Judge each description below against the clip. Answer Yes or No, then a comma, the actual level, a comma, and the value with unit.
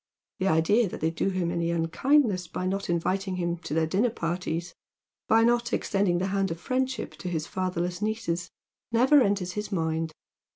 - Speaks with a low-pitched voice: No, medium, 185 Hz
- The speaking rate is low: No, average, 175 wpm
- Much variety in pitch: No, average, 3.6 semitones